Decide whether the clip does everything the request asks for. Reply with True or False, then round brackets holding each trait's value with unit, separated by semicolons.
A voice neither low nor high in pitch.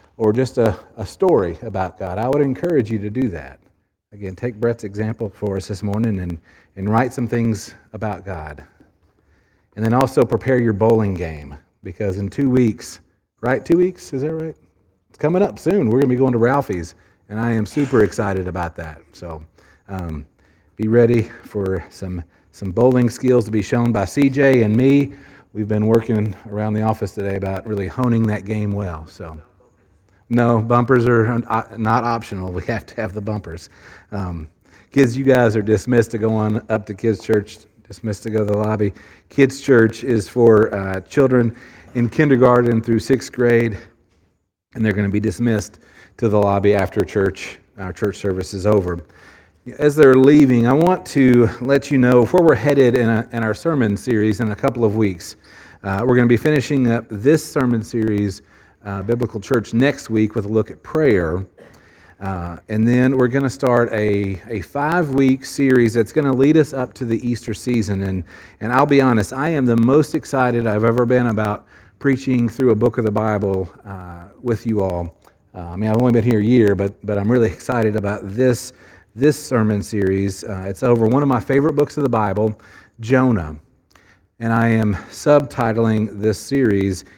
False (110 Hz)